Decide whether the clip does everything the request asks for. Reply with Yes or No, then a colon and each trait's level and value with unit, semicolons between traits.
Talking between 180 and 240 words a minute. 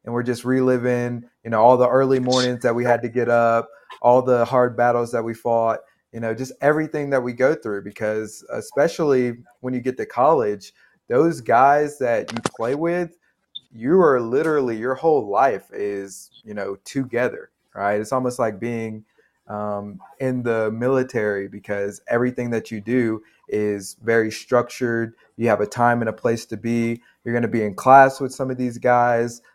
Yes: average, 185 wpm